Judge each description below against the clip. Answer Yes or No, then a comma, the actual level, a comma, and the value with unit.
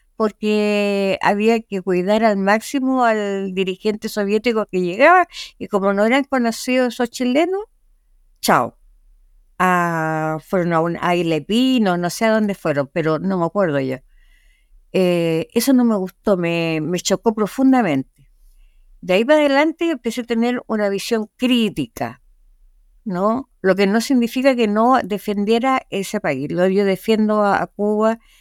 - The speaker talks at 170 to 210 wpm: No, average, 145 wpm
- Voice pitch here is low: No, high, 205 Hz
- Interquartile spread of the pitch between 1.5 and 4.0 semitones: No, average, 4.8 semitones